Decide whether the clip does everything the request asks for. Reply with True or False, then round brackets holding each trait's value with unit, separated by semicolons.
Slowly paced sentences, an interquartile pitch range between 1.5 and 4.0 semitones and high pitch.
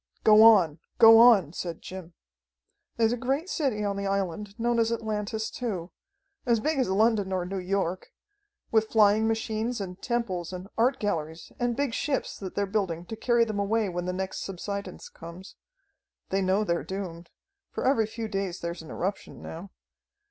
False (175 wpm; 3.6 semitones; 205 Hz)